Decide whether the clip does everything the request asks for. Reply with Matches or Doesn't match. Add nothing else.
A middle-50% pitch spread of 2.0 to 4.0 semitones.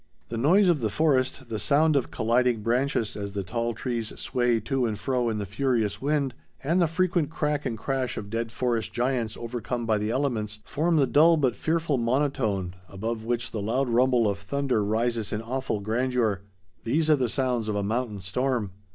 Matches